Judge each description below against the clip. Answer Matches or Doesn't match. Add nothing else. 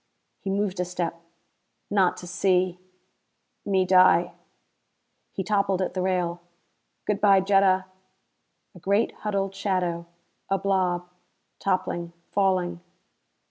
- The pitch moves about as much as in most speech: Doesn't match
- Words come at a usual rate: Doesn't match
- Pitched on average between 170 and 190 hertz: Matches